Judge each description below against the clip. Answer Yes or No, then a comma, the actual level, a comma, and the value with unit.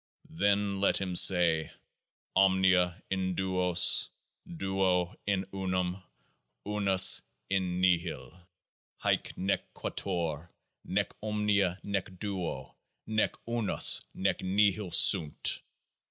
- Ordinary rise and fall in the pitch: No, narrow, 1.7 semitones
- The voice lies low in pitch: Yes, very low, 95 Hz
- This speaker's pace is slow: Yes, slow, 95 wpm